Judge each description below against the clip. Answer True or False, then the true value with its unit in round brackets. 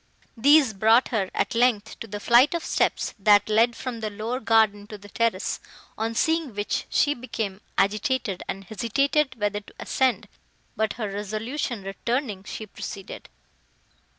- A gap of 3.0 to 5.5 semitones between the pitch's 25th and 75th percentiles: True (3.3 semitones)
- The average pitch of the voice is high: True (220 Hz)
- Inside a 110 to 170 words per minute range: True (150 wpm)